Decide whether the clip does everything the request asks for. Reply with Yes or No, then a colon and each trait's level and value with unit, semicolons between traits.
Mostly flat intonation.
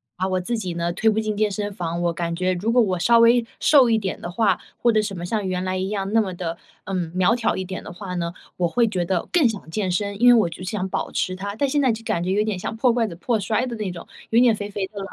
No: average, 3.6 semitones